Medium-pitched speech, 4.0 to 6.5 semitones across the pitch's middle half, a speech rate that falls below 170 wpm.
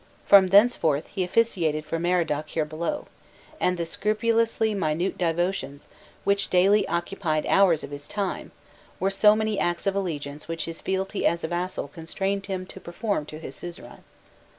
No: medium, 180 Hz; average, 3.4 semitones; average, 160 wpm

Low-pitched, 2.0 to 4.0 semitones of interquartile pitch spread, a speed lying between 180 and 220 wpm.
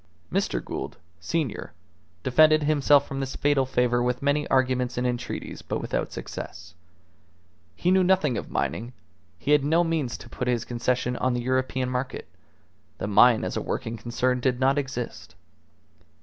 No: low, 130 Hz; average, 2.8 semitones; average, 160 wpm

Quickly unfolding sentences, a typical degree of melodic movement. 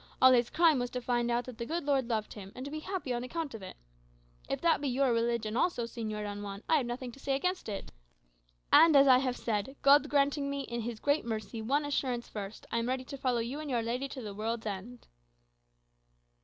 Yes: fast, 235 wpm; average, 3.4 semitones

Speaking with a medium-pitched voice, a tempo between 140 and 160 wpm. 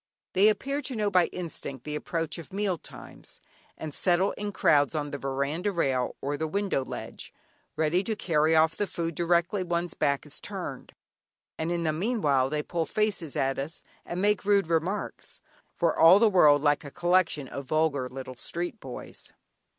No: medium, 165 Hz; average, 180 wpm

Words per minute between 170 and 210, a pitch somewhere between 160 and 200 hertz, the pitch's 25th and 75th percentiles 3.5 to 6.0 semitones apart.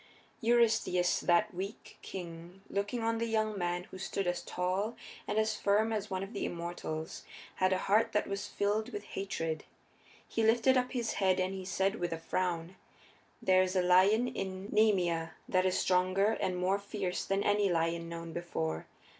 No: average, 180 wpm; high, 190 Hz; average, 3.0 semitones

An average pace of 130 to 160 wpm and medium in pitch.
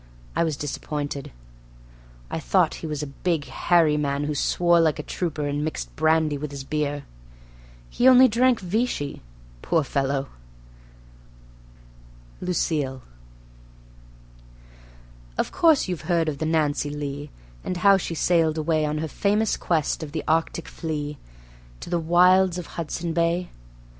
Yes: average, 140 wpm; medium, 160 Hz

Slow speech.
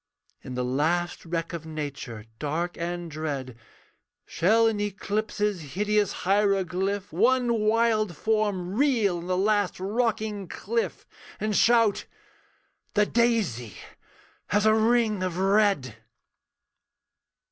Yes: slow, 110 wpm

